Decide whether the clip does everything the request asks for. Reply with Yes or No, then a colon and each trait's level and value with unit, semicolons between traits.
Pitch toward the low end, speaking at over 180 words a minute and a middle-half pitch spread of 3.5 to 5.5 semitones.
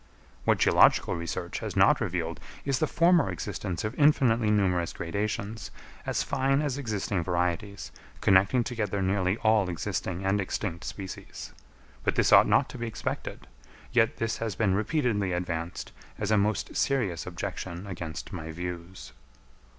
No: low, 100 Hz; average, 145 wpm; average, 4.2 semitones